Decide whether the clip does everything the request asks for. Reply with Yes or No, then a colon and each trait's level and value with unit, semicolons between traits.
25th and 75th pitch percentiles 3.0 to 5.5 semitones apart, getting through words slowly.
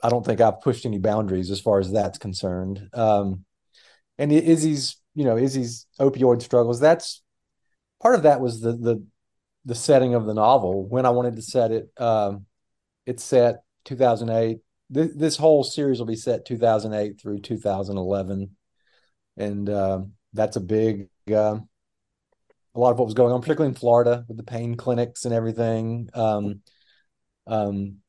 No: average, 3.4 semitones; average, 160 wpm